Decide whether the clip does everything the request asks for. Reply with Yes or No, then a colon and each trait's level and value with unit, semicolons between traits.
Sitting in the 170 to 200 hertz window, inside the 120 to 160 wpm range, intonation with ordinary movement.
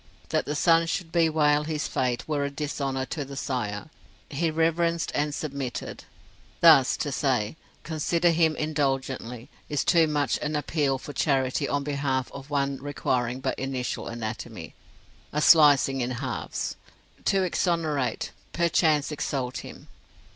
No: medium, 145 Hz; average, 140 wpm; average, 3.0 semitones